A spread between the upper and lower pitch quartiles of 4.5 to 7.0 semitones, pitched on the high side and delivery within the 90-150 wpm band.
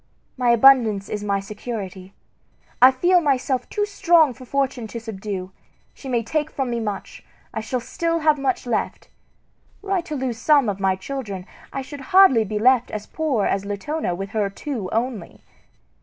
No: average, 5.2 semitones; high, 245 Hz; average, 175 wpm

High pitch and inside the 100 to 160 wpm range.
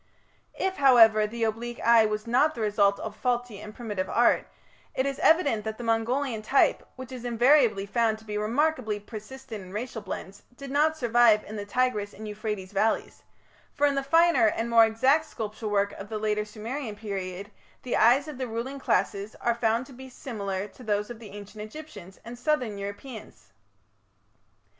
No: high, 225 Hz; average, 180 wpm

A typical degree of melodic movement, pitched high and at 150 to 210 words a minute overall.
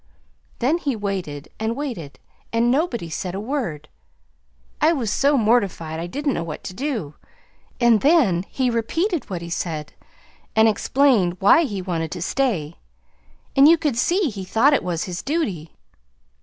No: wide, 8.0 semitones; high, 220 Hz; average, 160 wpm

